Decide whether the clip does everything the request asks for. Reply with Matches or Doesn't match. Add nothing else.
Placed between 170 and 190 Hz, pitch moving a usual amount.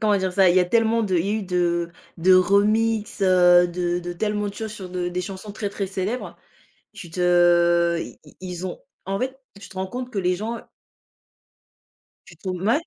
Matches